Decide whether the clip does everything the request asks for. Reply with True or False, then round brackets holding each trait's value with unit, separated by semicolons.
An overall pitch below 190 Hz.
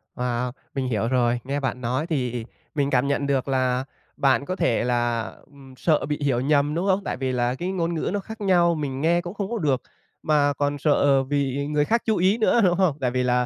True (140 Hz)